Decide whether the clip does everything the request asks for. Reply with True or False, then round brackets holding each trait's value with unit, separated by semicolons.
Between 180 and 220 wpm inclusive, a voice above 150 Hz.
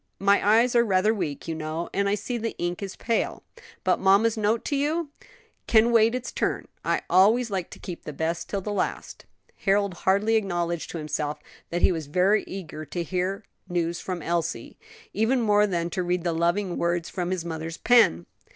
True (195 wpm; 190 Hz)